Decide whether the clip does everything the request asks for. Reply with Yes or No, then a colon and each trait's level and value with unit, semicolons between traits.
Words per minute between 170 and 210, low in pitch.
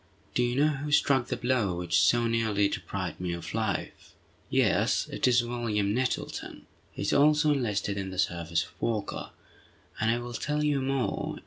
Yes: average, 180 wpm; low, 120 Hz